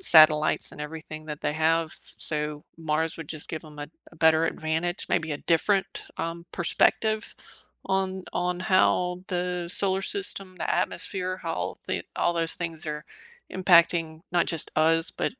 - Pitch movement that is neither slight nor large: No, narrow, 2.3 semitones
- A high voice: No, medium, 165 Hz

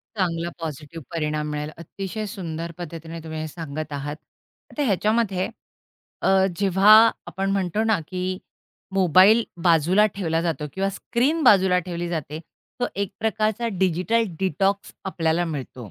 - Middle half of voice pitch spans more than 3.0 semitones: Yes, average, 3.7 semitones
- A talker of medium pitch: Yes, medium, 180 Hz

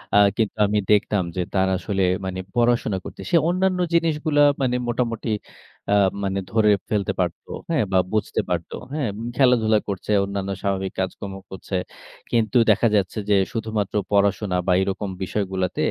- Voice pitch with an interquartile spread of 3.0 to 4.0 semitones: Yes, average, 3.6 semitones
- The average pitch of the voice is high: No, low, 105 Hz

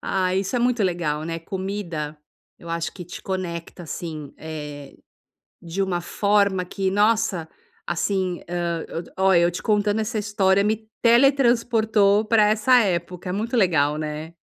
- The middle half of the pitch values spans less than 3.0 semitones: No, average, 3.8 semitones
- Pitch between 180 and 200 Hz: Yes, high, 190 Hz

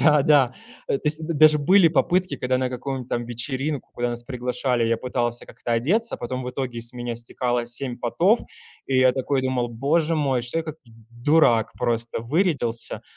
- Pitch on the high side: No, low, 130 Hz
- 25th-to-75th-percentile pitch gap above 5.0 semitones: No, average, 3.9 semitones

